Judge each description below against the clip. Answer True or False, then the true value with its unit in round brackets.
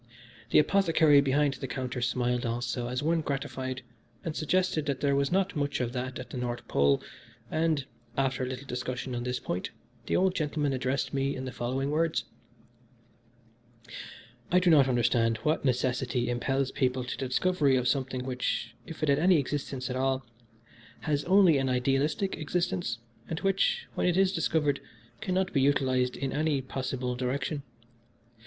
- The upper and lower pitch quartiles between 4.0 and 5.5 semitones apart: False (3.5 semitones)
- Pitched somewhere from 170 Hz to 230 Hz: False (135 Hz)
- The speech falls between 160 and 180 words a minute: True (165 wpm)